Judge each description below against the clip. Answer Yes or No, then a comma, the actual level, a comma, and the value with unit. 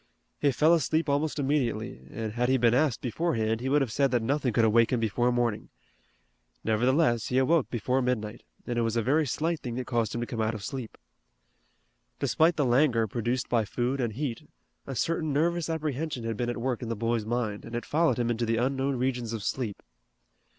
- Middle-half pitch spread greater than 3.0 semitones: Yes, average, 3.5 semitones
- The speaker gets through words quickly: Yes, fast, 210 wpm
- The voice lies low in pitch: Yes, low, 125 Hz